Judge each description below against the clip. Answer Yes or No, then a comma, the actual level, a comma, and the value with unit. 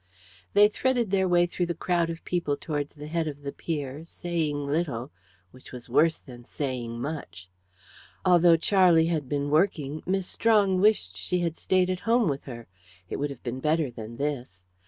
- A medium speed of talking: Yes, average, 180 wpm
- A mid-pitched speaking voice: Yes, medium, 155 Hz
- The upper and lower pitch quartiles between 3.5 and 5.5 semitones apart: Yes, average, 4.5 semitones